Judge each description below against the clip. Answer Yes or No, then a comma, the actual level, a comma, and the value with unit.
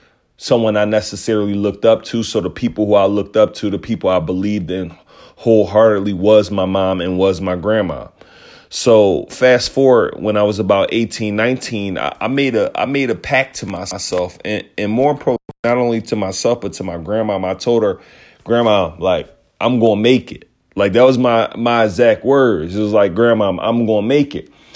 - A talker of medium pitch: No, low, 110 Hz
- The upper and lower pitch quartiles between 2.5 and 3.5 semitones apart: Yes, average, 2.8 semitones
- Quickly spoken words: No, average, 195 wpm